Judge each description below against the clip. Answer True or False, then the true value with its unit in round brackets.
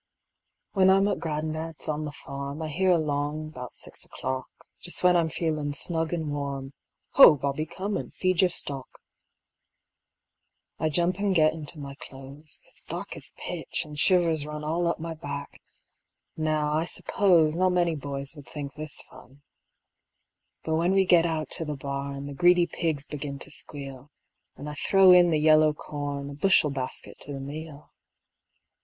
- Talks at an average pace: True (170 wpm)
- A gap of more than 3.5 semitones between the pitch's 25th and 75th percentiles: False (3.0 semitones)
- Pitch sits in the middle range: True (155 Hz)